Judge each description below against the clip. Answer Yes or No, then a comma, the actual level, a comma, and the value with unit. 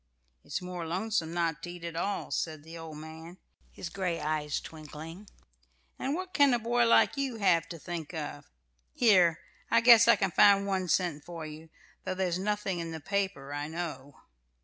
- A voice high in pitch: No, medium, 175 Hz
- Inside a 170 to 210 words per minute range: Yes, average, 185 wpm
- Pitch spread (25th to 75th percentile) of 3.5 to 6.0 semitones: Yes, average, 3.9 semitones